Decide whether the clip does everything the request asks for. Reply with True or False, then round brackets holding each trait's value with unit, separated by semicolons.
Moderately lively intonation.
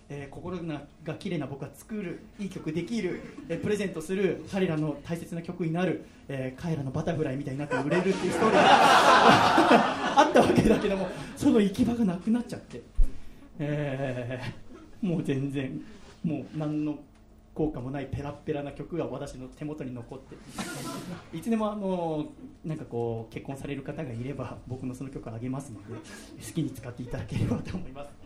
True (4.6 semitones)